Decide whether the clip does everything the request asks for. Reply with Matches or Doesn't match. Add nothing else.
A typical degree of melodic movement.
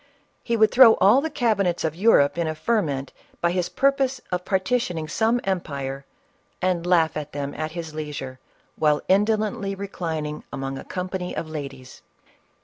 Doesn't match